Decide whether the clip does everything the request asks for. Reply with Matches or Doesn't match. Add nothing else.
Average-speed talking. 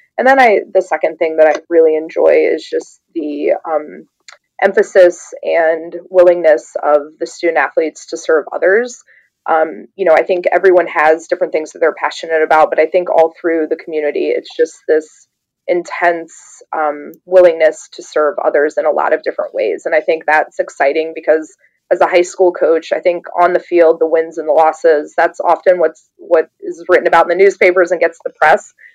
Matches